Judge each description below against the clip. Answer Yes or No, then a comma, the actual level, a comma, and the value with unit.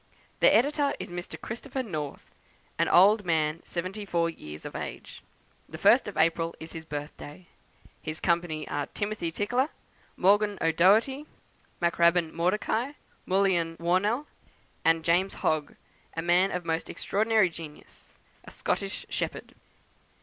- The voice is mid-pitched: Yes, medium, 175 Hz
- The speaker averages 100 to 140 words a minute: Yes, slow, 135 wpm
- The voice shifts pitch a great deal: No, average, 4.0 semitones